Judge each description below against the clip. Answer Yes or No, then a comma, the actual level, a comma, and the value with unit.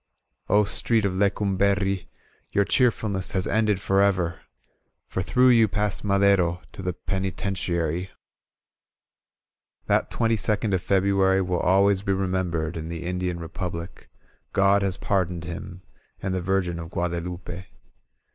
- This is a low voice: Yes, very low, 95 Hz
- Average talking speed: No, slow, 130 wpm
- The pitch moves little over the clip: Yes, narrow, 2.1 semitones